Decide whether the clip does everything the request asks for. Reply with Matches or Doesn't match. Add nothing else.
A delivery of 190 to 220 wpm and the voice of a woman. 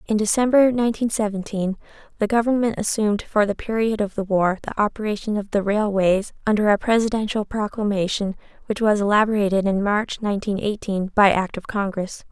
Doesn't match